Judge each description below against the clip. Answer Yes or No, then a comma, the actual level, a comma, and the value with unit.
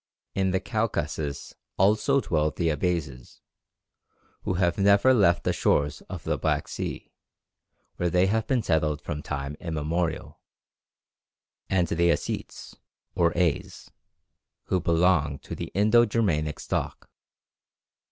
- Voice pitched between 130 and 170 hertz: No, very low, 85 Hz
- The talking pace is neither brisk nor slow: No, slow, 125 wpm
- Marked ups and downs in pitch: No, average, 4.4 semitones